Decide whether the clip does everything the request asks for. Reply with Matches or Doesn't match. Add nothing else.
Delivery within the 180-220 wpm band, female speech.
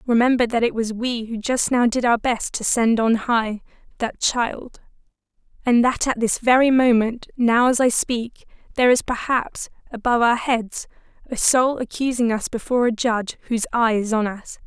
Matches